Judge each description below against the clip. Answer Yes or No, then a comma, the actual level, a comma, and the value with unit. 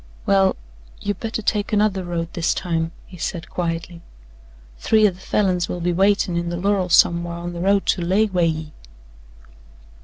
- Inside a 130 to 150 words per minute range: No, average, 175 wpm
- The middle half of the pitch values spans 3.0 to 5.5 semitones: No, narrow, 2.6 semitones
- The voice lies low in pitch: No, medium, 180 Hz